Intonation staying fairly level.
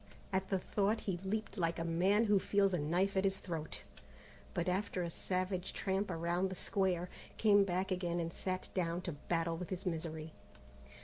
Yes: narrow, 2.3 semitones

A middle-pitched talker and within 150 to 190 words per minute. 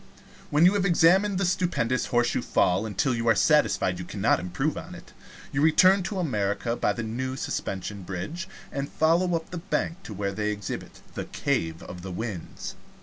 No: low, 125 Hz; average, 185 wpm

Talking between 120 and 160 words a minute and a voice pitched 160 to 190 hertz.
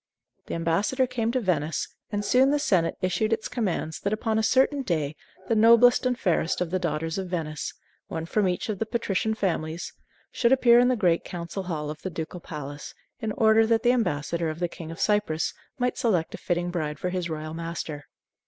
No: fast, 205 wpm; medium, 185 Hz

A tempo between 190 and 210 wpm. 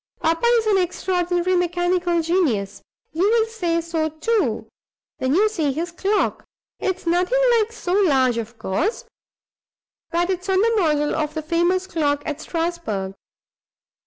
No: average, 145 wpm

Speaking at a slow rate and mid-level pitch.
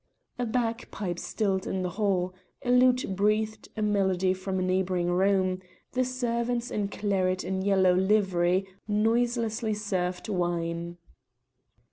No: slow, 125 wpm; high, 195 Hz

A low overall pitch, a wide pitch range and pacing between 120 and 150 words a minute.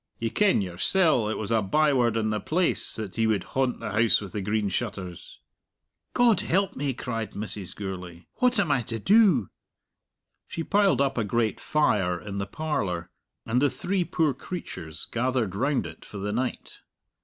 No: low, 115 Hz; wide, 7.0 semitones; average, 180 wpm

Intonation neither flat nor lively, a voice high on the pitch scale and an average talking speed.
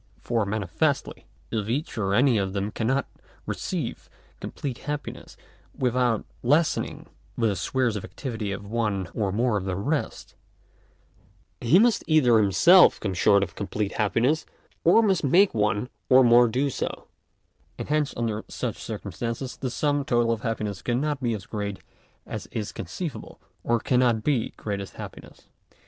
No: average, 4.6 semitones; low, 115 Hz; average, 150 wpm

